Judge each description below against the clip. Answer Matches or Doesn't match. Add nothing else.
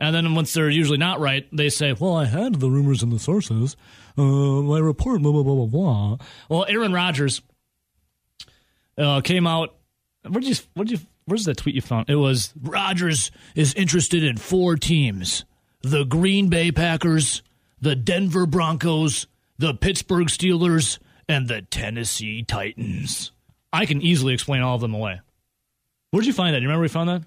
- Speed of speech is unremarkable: Matches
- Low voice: Doesn't match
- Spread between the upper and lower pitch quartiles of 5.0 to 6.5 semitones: Matches